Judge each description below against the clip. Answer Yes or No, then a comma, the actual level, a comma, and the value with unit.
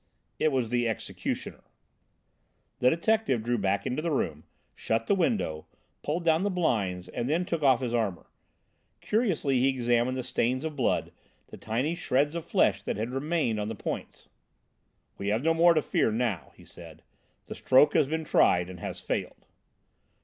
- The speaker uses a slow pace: No, average, 175 wpm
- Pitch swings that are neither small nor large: No, wide, 6.0 semitones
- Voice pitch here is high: No, low, 130 Hz